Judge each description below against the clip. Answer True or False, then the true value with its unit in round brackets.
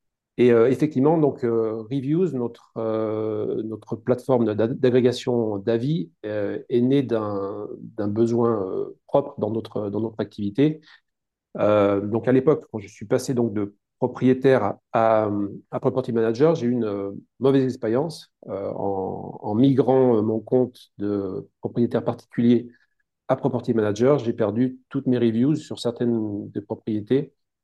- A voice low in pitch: True (115 Hz)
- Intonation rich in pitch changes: False (3.2 semitones)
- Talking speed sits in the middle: False (130 wpm)